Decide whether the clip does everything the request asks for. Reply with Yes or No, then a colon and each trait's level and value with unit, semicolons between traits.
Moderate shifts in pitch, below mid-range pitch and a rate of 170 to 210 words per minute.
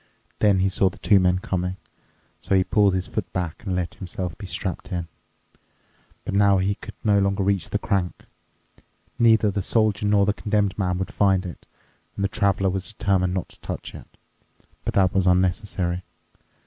No: narrow, 1.7 semitones; very low, 95 Hz; average, 185 wpm